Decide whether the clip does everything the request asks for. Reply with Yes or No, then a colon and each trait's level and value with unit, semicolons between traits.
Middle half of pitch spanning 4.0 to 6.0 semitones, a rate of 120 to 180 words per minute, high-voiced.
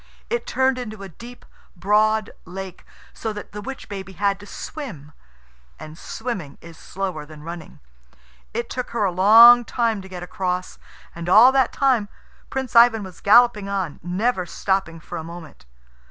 Yes: average, 4.9 semitones; average, 165 wpm; high, 200 Hz